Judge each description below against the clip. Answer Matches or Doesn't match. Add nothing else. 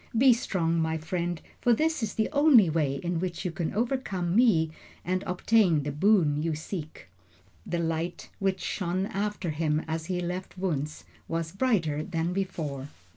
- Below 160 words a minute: Doesn't match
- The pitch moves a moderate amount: Matches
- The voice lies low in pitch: Doesn't match